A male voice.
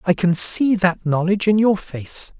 Yes: male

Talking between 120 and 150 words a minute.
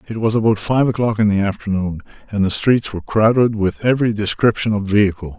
No: average, 200 wpm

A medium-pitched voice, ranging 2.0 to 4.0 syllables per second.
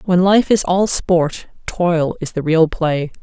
Yes: medium, 170 Hz; 3.5 syllables/s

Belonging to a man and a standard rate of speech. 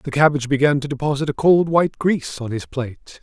No: male; fast, 225 wpm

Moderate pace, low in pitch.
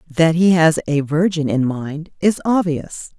No: average, 170 wpm; medium, 160 Hz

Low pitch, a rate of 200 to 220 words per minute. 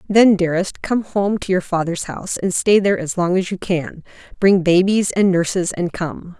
No: medium, 185 Hz; fast, 205 wpm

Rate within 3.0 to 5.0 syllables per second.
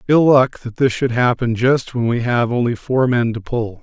Yes: 4.6 syllables/s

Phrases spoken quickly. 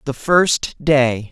No: slow, 135 wpm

